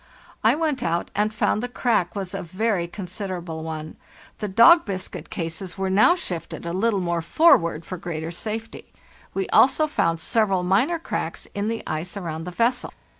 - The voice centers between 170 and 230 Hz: Yes, high, 190 Hz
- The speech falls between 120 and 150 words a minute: No, average, 175 wpm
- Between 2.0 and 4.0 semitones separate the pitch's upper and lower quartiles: No, average, 4.9 semitones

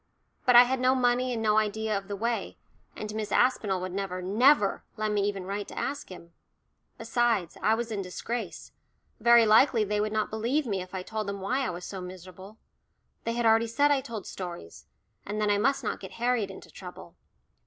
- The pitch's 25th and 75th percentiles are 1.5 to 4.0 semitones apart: Yes, average, 3.5 semitones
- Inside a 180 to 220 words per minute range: Yes, fast, 205 wpm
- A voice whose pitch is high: Yes, high, 215 Hz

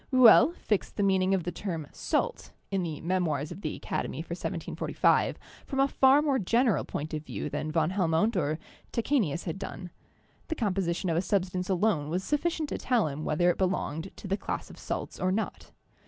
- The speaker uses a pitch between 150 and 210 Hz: Yes, medium, 185 Hz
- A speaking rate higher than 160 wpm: Yes, average, 195 wpm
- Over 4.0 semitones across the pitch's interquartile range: Yes, average, 5.0 semitones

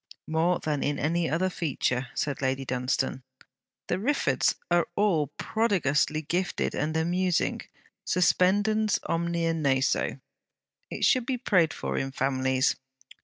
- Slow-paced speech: Yes, slow, 120 wpm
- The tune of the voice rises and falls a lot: No, average, 4.8 semitones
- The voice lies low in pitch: No, medium, 165 Hz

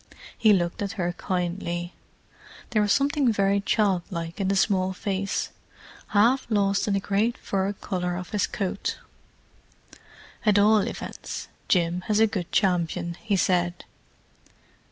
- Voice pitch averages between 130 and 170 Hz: No, high, 195 Hz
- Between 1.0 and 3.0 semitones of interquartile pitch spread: Yes, average, 2.7 semitones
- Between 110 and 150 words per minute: Yes, average, 140 wpm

